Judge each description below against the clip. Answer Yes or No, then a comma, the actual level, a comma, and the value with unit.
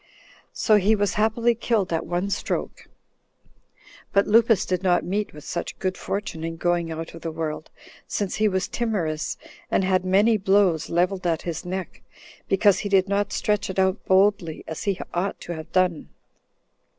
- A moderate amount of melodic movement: Yes, average, 3.0 semitones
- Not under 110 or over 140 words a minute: No, average, 175 wpm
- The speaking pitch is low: No, high, 190 Hz